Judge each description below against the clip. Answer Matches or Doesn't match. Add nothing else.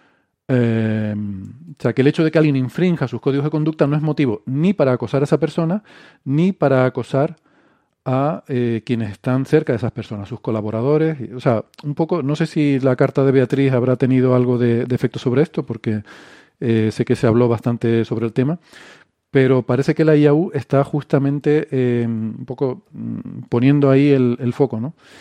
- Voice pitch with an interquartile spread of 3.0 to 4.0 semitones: Matches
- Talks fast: Matches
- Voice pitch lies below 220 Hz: Matches